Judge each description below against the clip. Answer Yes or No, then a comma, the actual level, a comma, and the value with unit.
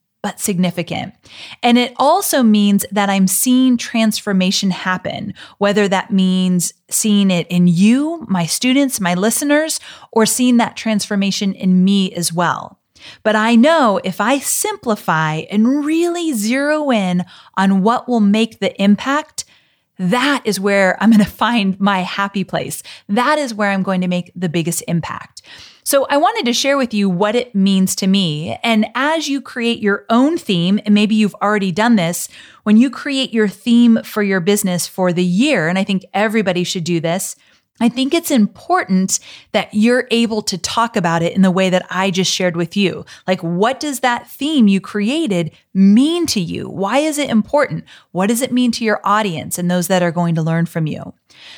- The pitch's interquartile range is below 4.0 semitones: No, average, 4.5 semitones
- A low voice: No, high, 205 Hz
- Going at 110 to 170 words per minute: No, average, 185 wpm